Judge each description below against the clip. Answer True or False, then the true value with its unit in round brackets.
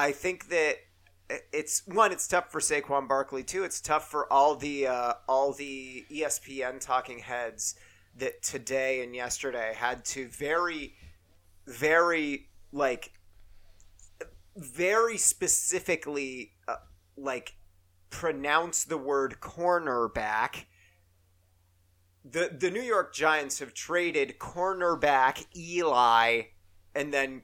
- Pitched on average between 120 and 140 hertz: True (135 Hz)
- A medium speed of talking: False (110 wpm)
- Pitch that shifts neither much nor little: False (6.9 semitones)